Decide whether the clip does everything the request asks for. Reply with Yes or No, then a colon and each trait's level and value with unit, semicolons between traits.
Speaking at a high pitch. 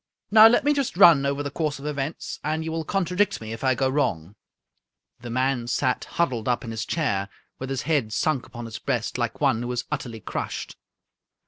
No: low, 135 Hz